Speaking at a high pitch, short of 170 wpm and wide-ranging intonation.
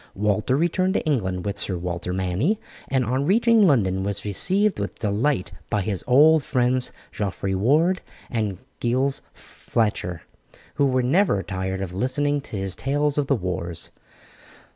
No: low, 120 Hz; average, 150 wpm; wide, 7.2 semitones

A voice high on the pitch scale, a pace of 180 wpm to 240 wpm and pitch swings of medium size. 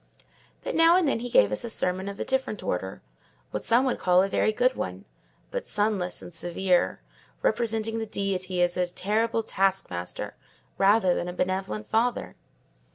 No: high, 195 Hz; average, 165 wpm; average, 4.2 semitones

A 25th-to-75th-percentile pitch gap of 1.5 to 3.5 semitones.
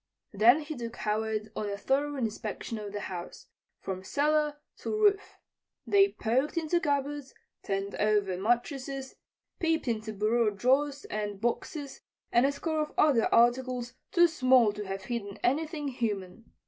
No: wide, 5.6 semitones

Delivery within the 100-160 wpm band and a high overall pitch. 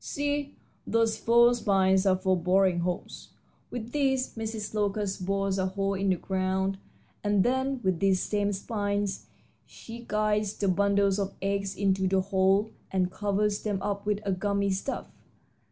Yes: average, 155 wpm; high, 200 Hz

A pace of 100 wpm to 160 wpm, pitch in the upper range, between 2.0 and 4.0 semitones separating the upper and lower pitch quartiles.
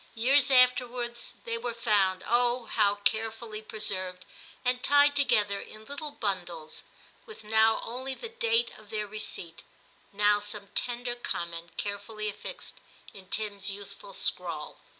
Yes: slow, 135 wpm; high, 220 Hz; average, 3.5 semitones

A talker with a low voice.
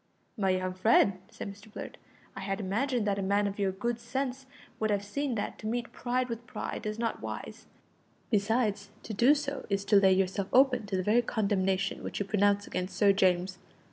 No: high, 205 Hz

